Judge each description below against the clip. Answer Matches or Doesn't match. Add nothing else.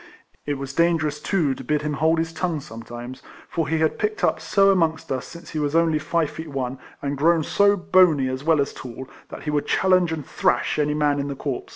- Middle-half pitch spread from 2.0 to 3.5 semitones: Matches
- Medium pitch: Matches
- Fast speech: Matches